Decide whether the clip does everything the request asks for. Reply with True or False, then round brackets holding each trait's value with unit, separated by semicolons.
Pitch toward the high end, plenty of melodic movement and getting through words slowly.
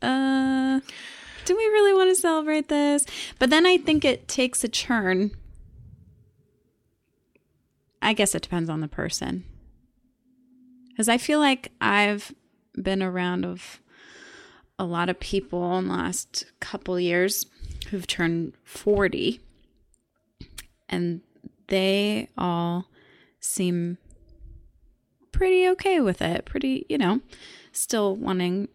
True (205 Hz; 7.2 semitones; 115 wpm)